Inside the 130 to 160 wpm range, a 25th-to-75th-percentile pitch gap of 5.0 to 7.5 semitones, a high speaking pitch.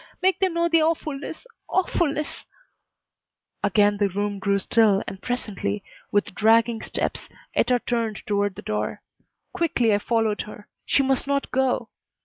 Yes: average, 145 wpm; wide, 5.4 semitones; high, 225 Hz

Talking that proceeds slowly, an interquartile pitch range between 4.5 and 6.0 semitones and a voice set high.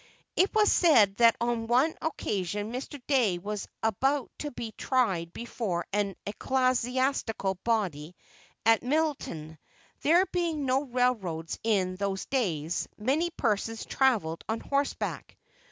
Yes: slow, 120 wpm; wide, 5.5 semitones; high, 230 Hz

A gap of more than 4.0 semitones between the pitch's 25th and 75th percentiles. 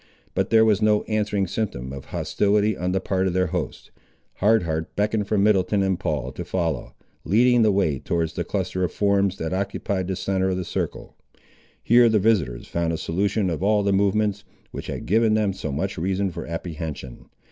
No: average, 3.5 semitones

